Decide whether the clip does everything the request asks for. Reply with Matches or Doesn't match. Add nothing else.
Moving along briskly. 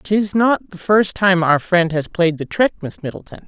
Matches